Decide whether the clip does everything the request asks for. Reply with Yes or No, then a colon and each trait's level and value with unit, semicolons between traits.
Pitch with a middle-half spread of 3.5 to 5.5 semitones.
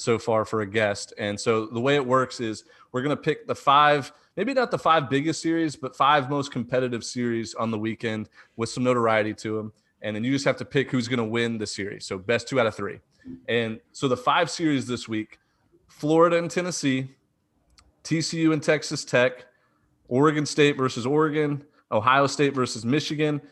Yes: average, 4.4 semitones